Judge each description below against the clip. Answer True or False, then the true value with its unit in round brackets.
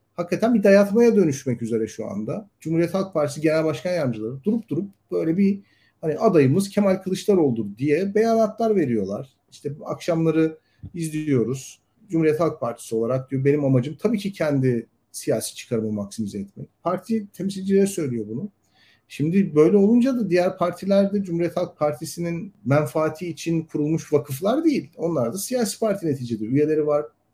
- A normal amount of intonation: False (6.3 semitones)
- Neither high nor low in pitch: True (160 Hz)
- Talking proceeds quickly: True (150 wpm)